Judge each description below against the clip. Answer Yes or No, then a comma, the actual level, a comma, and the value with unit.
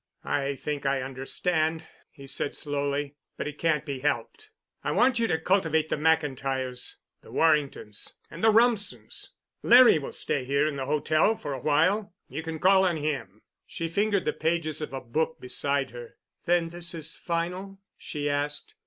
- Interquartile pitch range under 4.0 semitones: Yes, average, 3.5 semitones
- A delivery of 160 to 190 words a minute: Yes, average, 170 wpm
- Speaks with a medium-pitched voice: Yes, medium, 155 Hz